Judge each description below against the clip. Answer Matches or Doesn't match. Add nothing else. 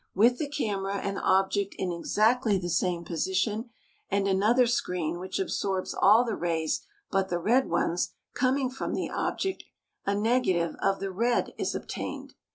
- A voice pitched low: Doesn't match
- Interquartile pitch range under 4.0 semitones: Doesn't match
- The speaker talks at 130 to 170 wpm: Matches